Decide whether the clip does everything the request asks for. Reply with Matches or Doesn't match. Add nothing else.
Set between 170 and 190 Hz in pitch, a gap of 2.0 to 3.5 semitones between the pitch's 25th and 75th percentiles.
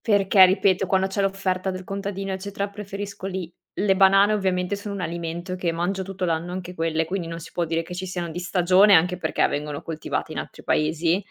Matches